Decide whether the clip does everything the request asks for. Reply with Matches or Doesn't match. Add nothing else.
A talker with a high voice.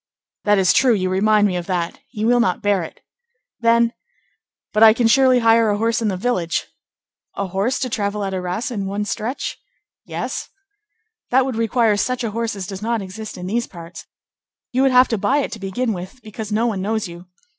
Matches